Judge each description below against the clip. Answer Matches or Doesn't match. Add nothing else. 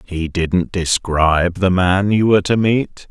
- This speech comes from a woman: Doesn't match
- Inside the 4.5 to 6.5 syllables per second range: Doesn't match